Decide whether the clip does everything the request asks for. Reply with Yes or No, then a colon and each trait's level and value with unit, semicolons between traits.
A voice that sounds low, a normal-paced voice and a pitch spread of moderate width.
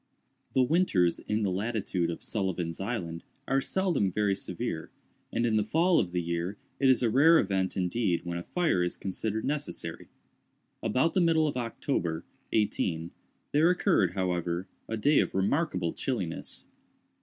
No: low, 105 Hz; average, 155 wpm; wide, 7.3 semitones